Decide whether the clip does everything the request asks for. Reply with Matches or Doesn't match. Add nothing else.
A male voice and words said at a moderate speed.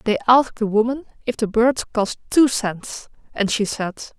Doesn't match